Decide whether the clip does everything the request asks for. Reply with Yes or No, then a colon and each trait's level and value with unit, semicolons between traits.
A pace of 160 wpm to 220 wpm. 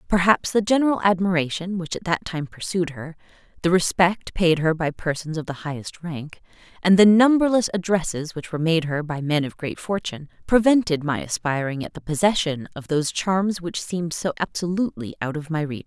Yes: average, 190 wpm